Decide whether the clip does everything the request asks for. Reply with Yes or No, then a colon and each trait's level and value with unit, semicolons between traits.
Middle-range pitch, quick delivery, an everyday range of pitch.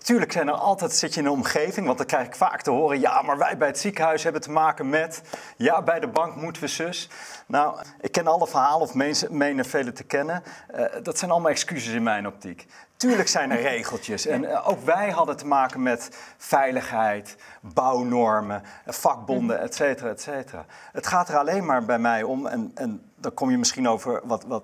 No: medium, 155 Hz; fast, 210 wpm; wide, 6.4 semitones